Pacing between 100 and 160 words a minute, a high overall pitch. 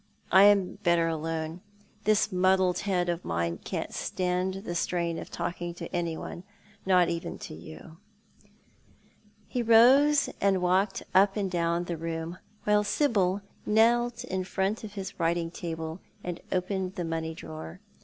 No: average, 150 wpm; medium, 180 Hz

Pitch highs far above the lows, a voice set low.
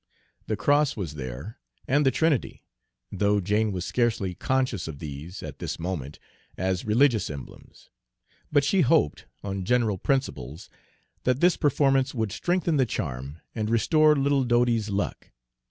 Yes: wide, 6.9 semitones; low, 110 Hz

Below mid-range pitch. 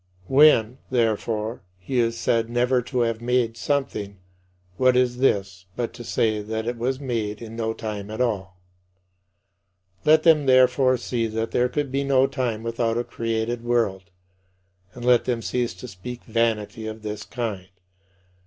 Yes: low, 115 Hz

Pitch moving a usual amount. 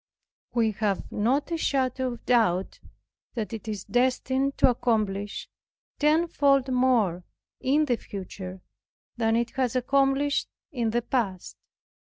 Yes: average, 3.9 semitones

